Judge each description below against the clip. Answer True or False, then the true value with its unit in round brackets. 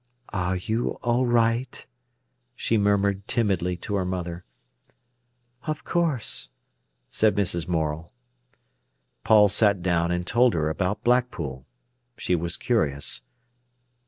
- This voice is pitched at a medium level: False (100 Hz)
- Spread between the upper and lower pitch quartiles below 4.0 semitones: False (4.9 semitones)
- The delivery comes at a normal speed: False (110 wpm)